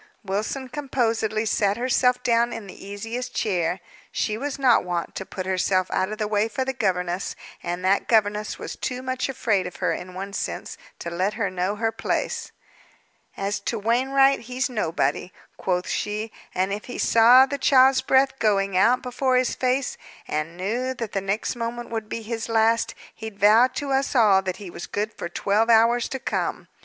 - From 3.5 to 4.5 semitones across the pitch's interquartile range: Yes, average, 4.2 semitones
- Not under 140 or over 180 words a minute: No, average, 190 wpm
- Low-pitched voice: No, high, 220 Hz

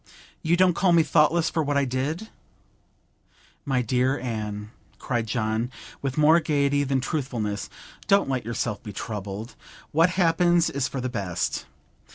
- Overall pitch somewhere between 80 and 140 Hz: Yes, low, 135 Hz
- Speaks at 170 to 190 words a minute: No, average, 150 wpm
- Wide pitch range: Yes, wide, 5.7 semitones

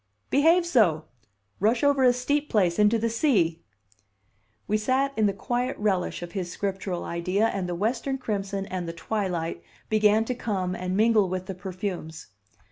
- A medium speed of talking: Yes, average, 165 wpm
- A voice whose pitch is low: No, high, 205 Hz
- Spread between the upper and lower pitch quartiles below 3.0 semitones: No, average, 4.3 semitones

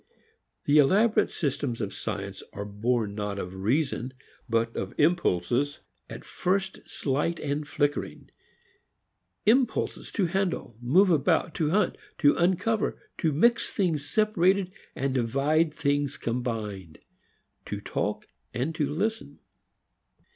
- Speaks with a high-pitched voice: No, medium, 145 Hz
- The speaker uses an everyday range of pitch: No, wide, 7.2 semitones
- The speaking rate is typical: No, slow, 120 wpm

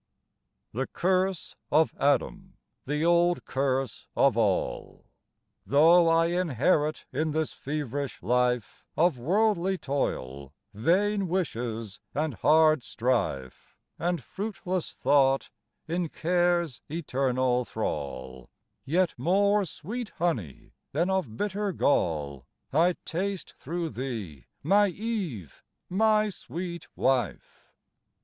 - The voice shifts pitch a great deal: Yes, wide, 6.3 semitones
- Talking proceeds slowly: Yes, slow, 100 wpm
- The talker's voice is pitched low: No, medium, 155 Hz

